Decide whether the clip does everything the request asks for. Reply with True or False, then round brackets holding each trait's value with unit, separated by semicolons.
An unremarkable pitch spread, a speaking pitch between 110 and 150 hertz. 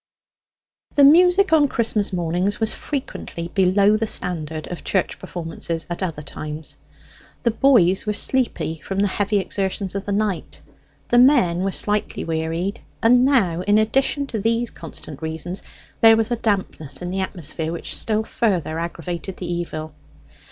False (4.8 semitones; 195 Hz)